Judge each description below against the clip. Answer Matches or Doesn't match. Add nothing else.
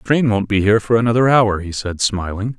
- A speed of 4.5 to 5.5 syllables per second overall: Doesn't match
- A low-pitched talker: Matches